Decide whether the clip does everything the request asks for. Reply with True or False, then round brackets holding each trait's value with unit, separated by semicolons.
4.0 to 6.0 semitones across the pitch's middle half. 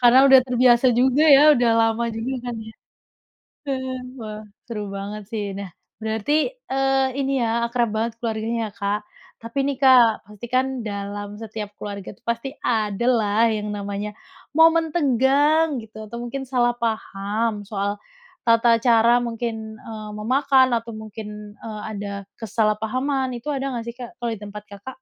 False (3.4 semitones)